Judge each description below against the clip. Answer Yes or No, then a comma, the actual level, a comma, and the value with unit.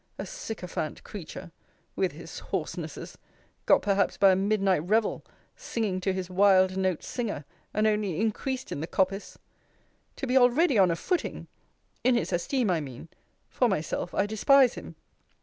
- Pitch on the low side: No, high, 200 Hz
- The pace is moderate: Yes, average, 155 wpm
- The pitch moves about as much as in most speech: Yes, average, 4.2 semitones